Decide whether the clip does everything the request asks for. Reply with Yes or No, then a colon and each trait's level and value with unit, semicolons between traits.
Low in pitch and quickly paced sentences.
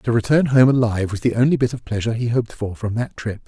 Yes: low, 115 Hz; fast, 275 wpm